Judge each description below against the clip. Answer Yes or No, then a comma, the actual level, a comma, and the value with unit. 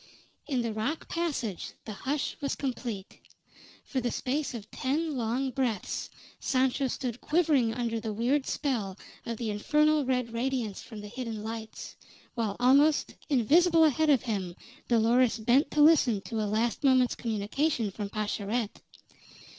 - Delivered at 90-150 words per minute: Yes, average, 145 wpm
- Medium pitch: No, high, 245 Hz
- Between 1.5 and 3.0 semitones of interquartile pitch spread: No, average, 3.9 semitones